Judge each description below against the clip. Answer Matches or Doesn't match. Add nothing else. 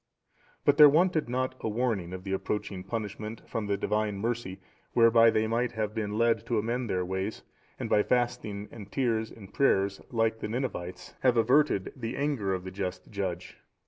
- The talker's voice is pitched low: Matches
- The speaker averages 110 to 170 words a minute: Doesn't match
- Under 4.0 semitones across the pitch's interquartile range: Matches